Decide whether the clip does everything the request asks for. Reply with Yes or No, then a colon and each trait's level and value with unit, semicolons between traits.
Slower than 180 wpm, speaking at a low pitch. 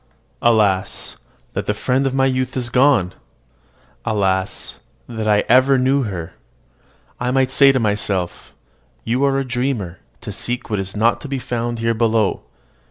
Yes: average, 160 wpm; low, 120 Hz